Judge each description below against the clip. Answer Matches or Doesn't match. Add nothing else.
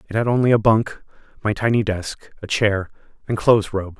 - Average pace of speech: Matches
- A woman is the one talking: Doesn't match